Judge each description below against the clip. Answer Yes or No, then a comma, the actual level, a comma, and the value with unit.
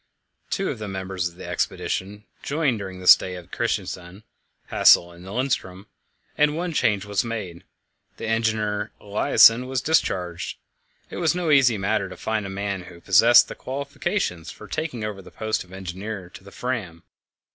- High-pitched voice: No, low, 105 Hz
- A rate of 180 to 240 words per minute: No, average, 170 wpm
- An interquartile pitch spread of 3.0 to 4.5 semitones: No, average, 4.9 semitones